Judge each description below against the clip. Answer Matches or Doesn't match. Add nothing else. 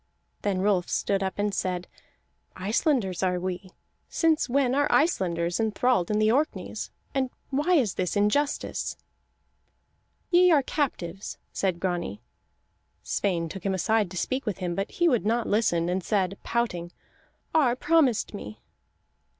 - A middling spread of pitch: Doesn't match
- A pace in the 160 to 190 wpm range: Doesn't match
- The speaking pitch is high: Matches